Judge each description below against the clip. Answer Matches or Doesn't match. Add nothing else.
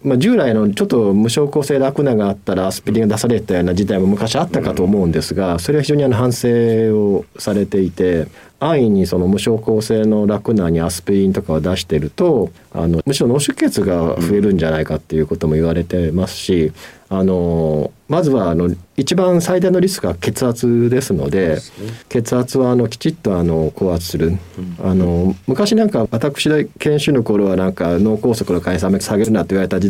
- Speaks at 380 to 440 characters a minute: Matches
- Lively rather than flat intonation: Matches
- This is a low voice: Matches